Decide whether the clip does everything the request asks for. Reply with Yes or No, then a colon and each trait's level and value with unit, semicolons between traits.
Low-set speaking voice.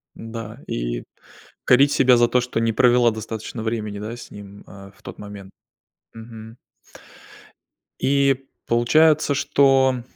Yes: low, 115 Hz